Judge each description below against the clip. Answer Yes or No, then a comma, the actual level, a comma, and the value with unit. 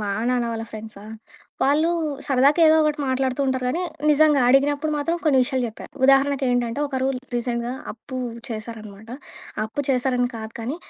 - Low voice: No, very high, 260 Hz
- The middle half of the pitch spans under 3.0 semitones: No, average, 3.4 semitones